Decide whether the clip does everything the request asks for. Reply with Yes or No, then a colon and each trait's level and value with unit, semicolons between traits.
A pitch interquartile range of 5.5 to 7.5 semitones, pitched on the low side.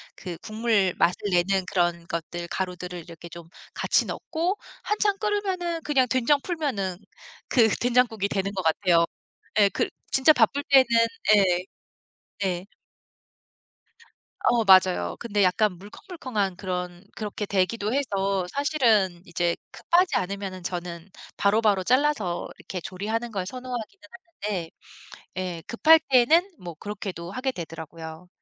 No: wide, 6.0 semitones; high, 200 Hz